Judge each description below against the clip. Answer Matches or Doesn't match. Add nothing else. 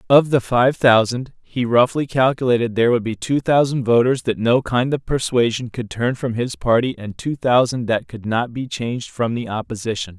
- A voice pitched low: Matches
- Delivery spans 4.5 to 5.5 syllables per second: Matches